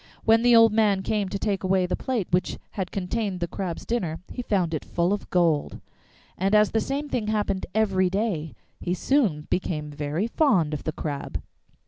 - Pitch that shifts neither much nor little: Yes, average, 4.2 semitones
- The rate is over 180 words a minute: Yes, average, 190 wpm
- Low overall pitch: No, high, 190 Hz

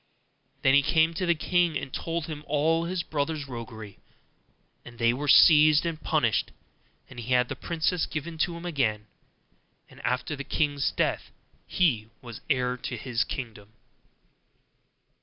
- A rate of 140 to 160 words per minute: Yes, average, 155 wpm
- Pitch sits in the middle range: Yes, medium, 145 Hz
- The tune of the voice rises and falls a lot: No, average, 4.8 semitones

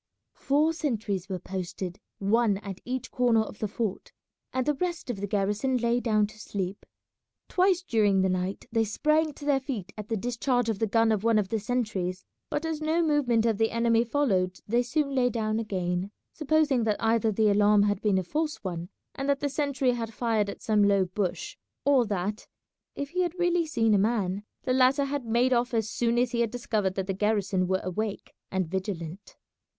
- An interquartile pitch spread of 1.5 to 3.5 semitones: No, average, 4.4 semitones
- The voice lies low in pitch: No, high, 225 Hz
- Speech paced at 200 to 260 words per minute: Yes, fast, 205 wpm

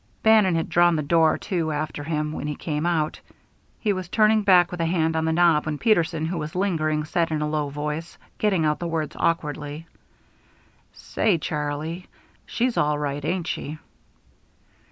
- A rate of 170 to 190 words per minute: Yes, average, 175 wpm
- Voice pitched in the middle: Yes, medium, 160 Hz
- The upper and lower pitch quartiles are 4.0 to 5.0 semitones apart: No, narrow, 2.5 semitones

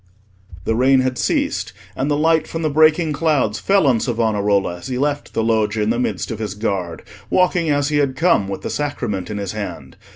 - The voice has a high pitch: No, low, 125 Hz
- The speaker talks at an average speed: No, fast, 215 wpm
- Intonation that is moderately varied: No, wide, 5.8 semitones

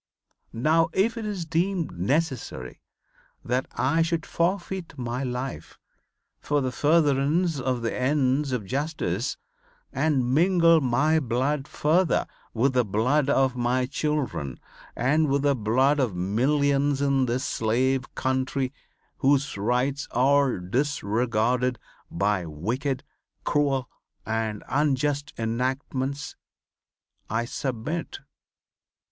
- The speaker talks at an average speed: No, slow, 110 wpm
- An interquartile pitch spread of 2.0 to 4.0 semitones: Yes, average, 3.4 semitones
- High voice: No, low, 135 Hz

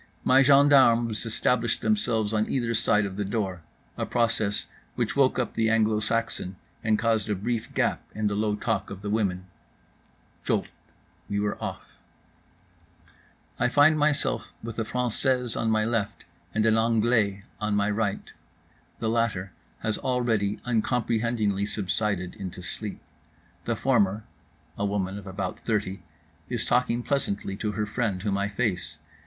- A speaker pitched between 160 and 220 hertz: No, low, 110 Hz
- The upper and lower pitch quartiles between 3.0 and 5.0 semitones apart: No, narrow, 2.5 semitones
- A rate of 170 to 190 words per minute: No, average, 150 wpm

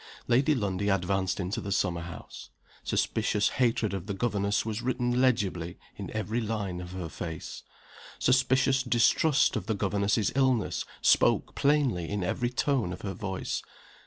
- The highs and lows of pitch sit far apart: No, average, 4.7 semitones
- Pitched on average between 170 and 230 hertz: No, low, 105 Hz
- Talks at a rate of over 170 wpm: No, average, 150 wpm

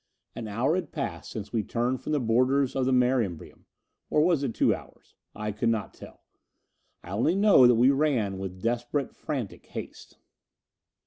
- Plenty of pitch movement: No, average, 4.1 semitones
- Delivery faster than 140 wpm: Yes, average, 180 wpm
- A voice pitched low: Yes, low, 125 Hz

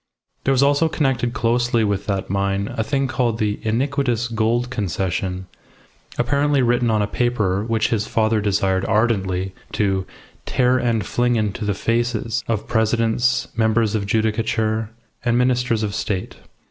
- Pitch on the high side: No, low, 115 Hz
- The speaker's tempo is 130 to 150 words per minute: Yes, average, 145 wpm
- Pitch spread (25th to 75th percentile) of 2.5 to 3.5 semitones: Yes, average, 2.8 semitones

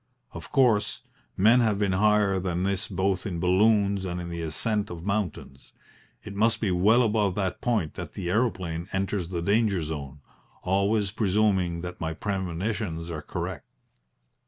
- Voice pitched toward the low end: Yes, very low, 95 Hz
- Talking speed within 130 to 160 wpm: Yes, average, 155 wpm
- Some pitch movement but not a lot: Yes, average, 3.3 semitones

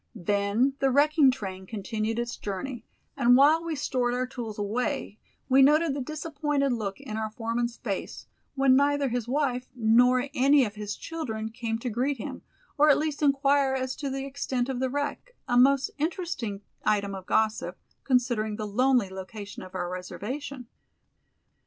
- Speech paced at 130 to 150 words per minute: No, average, 165 wpm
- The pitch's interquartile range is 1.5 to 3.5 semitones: No, average, 4.2 semitones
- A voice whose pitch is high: Yes, very high, 250 Hz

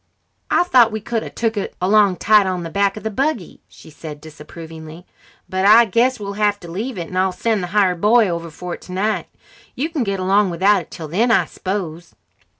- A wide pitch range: No, average, 3.9 semitones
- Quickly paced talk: Yes, fast, 220 wpm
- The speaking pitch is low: No, high, 195 Hz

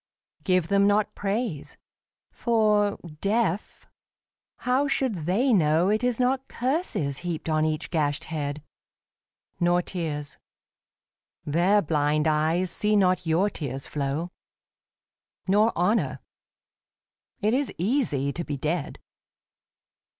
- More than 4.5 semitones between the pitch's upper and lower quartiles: Yes, wide, 5.6 semitones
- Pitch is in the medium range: Yes, medium, 180 Hz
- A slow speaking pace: Yes, slow, 110 wpm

